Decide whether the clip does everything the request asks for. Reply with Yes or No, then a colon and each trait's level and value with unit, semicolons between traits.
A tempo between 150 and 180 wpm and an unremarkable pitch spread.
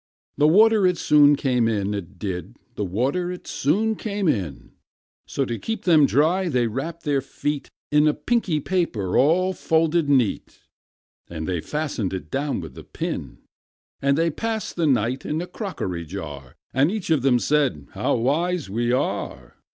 No: average, 170 wpm; wide, 7.4 semitones